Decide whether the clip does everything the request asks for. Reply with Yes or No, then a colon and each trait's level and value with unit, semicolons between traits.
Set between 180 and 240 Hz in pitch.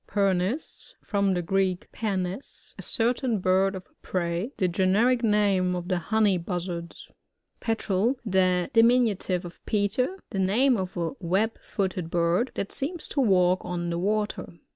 Yes: high, 190 Hz